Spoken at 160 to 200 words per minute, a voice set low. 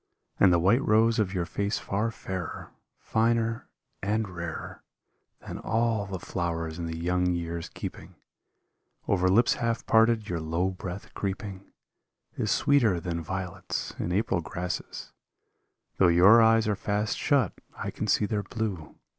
No: average, 145 wpm; very low, 95 Hz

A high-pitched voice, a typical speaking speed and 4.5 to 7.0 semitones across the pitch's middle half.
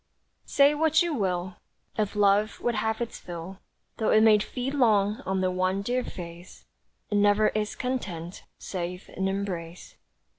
No: high, 205 Hz; average, 155 wpm; average, 3.5 semitones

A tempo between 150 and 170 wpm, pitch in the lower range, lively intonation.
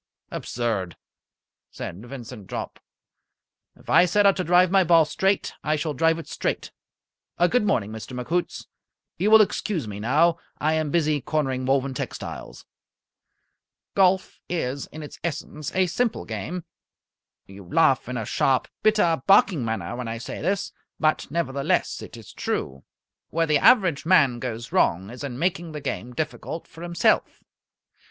No: average, 155 wpm; medium, 155 Hz; wide, 5.9 semitones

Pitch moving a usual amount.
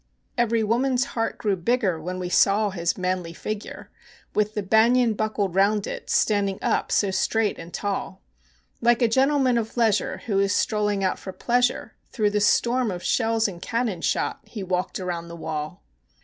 Yes: average, 3.6 semitones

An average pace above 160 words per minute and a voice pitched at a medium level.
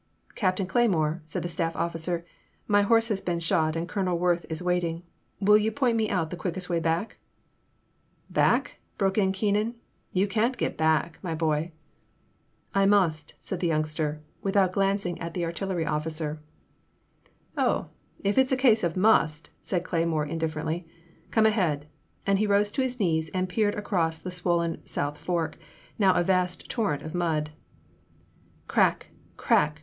Yes: average, 175 wpm; medium, 175 Hz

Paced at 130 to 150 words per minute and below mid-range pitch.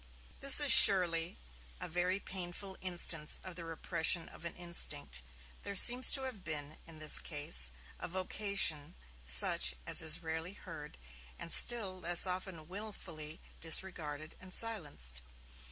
No: slow, 135 wpm; medium, 170 Hz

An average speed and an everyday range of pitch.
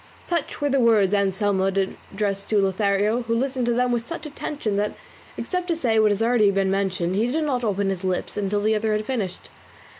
No: fast, 210 wpm; average, 3.7 semitones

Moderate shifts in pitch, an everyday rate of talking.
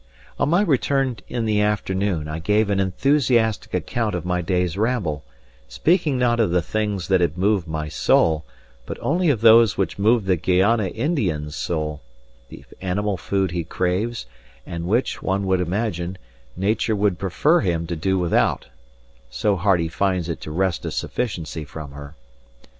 Yes: average, 4.5 semitones; average, 165 wpm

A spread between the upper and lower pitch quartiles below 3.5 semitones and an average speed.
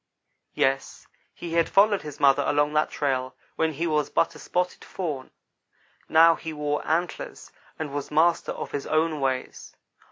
Yes: narrow, 2.6 semitones; average, 160 wpm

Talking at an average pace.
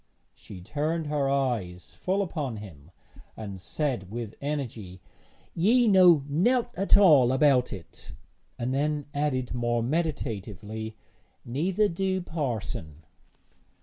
No: slow, 115 wpm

